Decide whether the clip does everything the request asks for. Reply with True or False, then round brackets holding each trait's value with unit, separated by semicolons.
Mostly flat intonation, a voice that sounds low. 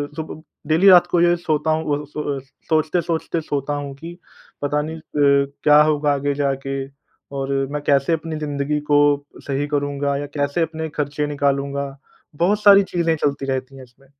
False (2.3 semitones; 150 Hz)